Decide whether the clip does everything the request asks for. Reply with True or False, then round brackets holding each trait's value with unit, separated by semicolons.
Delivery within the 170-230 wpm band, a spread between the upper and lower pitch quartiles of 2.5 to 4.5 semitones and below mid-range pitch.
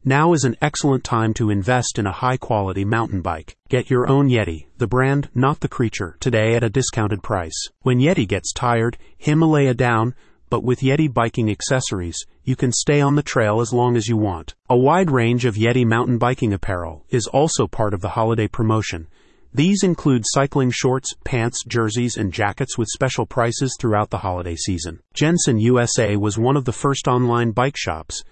True (190 wpm; 3.7 semitones; 120 Hz)